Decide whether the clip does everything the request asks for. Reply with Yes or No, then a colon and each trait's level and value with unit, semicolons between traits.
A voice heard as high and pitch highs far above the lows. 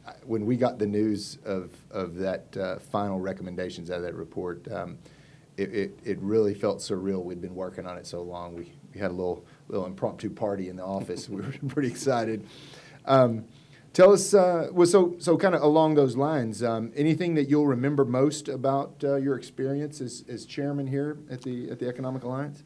No: low, 125 Hz; wide, 6.7 semitones